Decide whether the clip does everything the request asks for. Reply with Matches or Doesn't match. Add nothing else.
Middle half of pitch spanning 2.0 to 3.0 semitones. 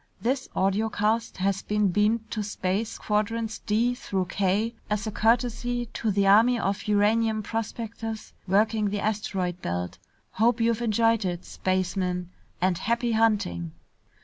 Matches